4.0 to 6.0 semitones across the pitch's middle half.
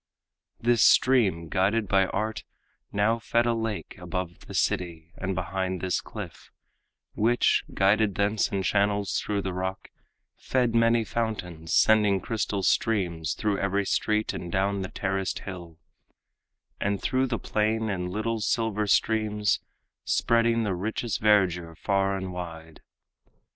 No: average, 3.1 semitones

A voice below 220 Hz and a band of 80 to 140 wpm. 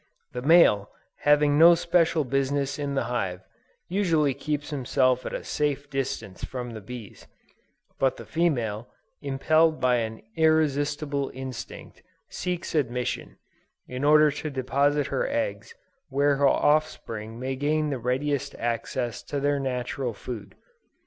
Yes: medium, 140 Hz; slow, 135 wpm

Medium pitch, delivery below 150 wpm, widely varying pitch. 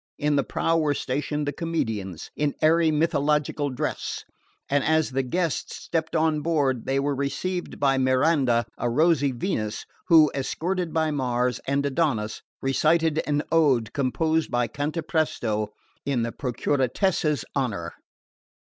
No: medium, 145 Hz; slow, 135 wpm; average, 3.7 semitones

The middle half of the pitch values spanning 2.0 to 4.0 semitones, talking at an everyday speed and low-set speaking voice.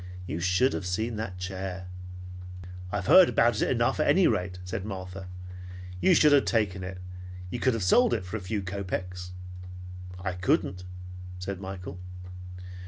Yes: average, 3.5 semitones; average, 160 wpm; very low, 95 Hz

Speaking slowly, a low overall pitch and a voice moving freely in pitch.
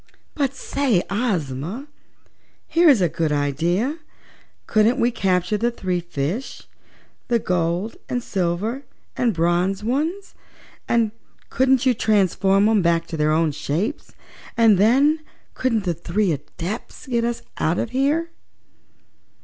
No: slow, 125 wpm; high, 210 Hz; wide, 6.3 semitones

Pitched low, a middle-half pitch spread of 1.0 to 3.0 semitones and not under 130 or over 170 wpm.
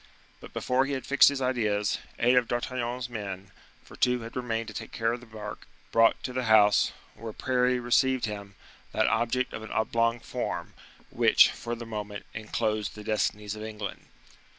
No: low, 115 Hz; narrow, 2.6 semitones; average, 180 wpm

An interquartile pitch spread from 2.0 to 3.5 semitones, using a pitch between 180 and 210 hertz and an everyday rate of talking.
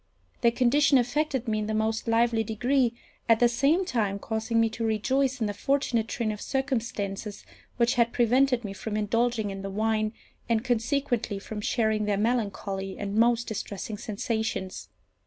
No: narrow, 2.4 semitones; high, 225 Hz; average, 165 wpm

